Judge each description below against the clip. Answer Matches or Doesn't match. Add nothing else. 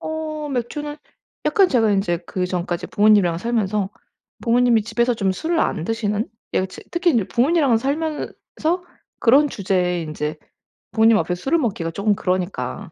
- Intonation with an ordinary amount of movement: Doesn't match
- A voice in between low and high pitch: Doesn't match